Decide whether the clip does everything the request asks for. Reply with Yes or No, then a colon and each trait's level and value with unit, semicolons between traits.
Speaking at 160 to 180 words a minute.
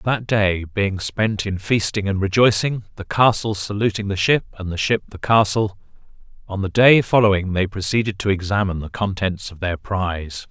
Yes: average, 175 wpm